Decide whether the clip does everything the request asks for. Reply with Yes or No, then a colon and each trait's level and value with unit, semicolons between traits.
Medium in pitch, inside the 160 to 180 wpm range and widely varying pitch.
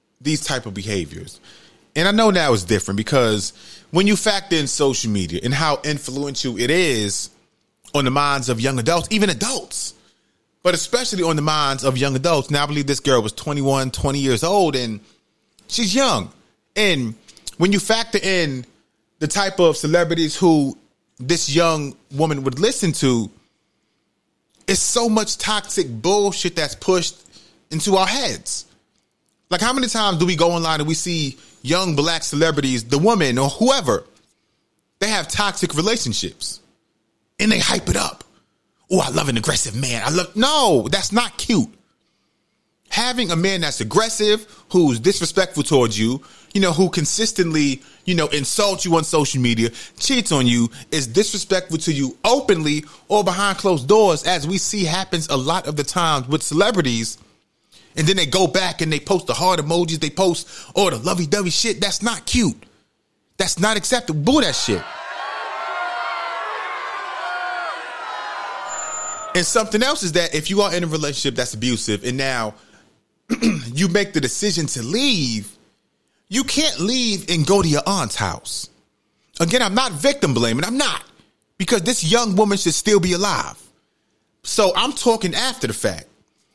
Yes: medium, 170 Hz; average, 165 wpm; wide, 6.7 semitones